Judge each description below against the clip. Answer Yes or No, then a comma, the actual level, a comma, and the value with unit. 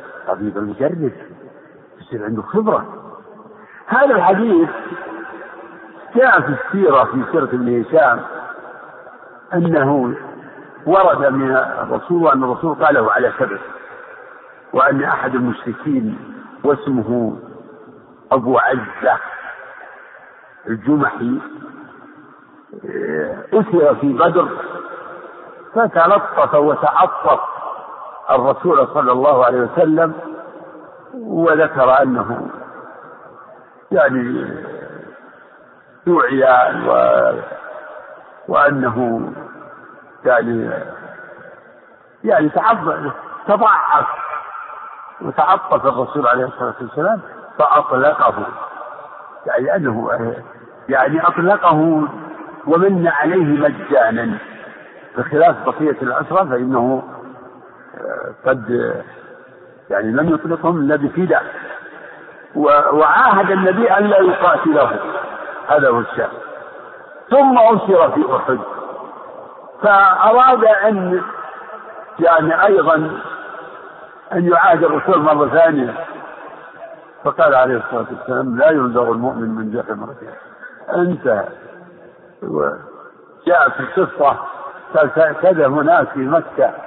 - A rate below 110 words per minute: Yes, average, 75 wpm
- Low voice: No, medium, 165 Hz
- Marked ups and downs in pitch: Yes, wide, 7.8 semitones